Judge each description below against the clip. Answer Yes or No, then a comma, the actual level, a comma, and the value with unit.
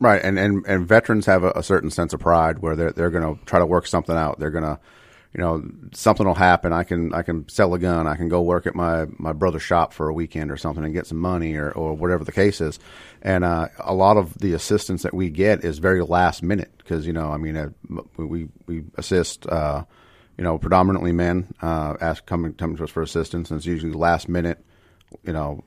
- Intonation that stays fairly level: Yes, narrow, 1.9 semitones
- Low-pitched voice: Yes, very low, 85 Hz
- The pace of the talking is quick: Yes, fast, 240 wpm